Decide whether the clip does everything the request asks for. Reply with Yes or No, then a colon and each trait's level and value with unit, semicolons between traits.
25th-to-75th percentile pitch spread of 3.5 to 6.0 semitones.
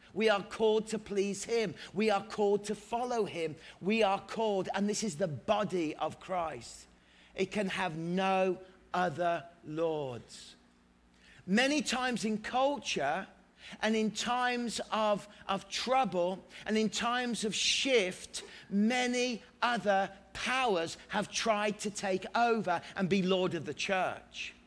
Yes: average, 3.9 semitones